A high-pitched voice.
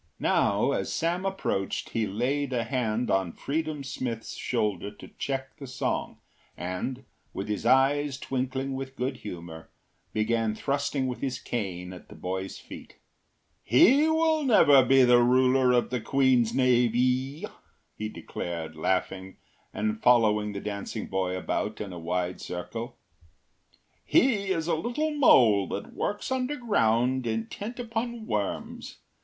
No: low, 125 Hz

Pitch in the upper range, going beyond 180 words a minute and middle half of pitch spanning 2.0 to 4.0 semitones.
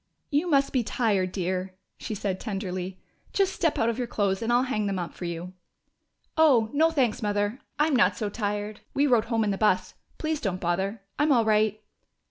No: high, 215 Hz; average, 200 wpm; average, 4.8 semitones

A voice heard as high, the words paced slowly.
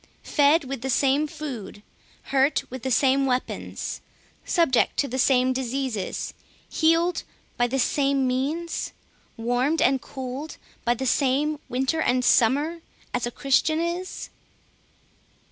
Yes: very high, 270 Hz; slow, 130 wpm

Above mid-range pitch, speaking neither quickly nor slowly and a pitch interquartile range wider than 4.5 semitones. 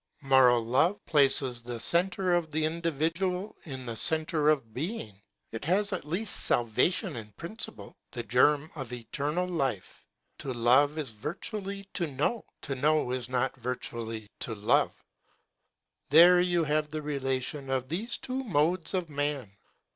No: medium, 150 Hz; average, 145 wpm; wide, 5.4 semitones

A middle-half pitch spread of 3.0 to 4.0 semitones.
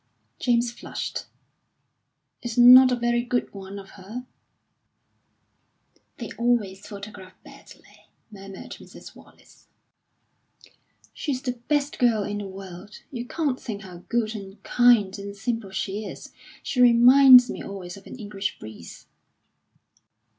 Yes: average, 3.7 semitones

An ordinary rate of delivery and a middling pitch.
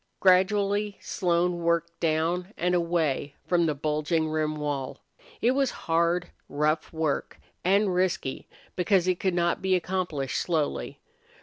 No: slow, 130 wpm; medium, 170 Hz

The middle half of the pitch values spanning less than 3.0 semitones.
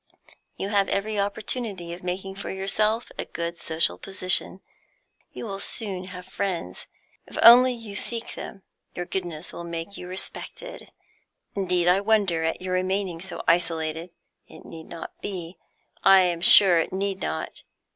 Yes: narrow, 2.6 semitones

